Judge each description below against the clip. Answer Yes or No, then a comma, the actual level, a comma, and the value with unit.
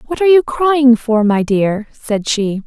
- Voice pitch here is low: No, high, 245 Hz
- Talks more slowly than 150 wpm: No, fast, 205 wpm